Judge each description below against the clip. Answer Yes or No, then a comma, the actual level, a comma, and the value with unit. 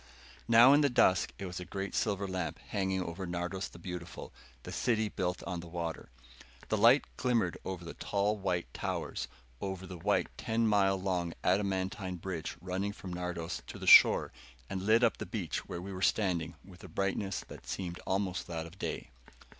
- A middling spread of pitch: No, narrow, 2.1 semitones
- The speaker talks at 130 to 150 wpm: No, average, 185 wpm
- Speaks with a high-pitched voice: No, very low, 95 Hz